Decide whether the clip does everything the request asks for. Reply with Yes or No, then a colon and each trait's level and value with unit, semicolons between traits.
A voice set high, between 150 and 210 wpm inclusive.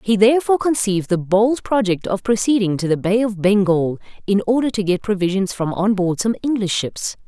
Yes: high, 205 Hz; average, 200 wpm